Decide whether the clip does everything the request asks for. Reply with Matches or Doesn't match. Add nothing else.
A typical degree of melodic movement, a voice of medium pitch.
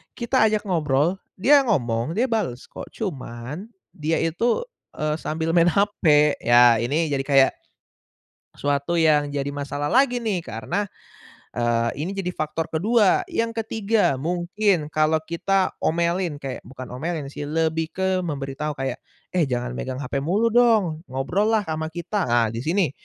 Doesn't match